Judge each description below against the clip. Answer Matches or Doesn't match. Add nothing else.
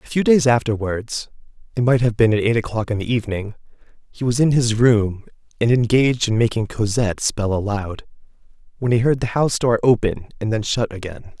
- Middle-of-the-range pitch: Doesn't match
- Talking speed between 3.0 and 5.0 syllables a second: Doesn't match